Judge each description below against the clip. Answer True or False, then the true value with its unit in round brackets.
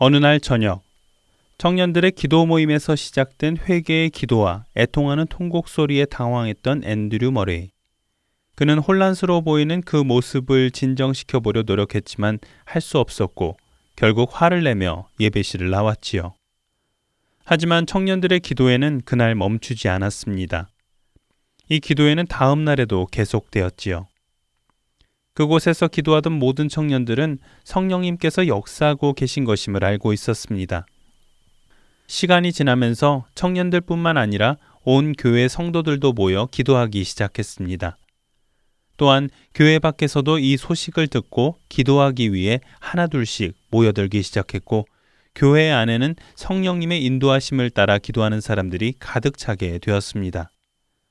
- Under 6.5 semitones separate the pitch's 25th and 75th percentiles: False (6.8 semitones)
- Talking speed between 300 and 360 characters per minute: True (305 characters per minute)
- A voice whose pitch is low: True (130 Hz)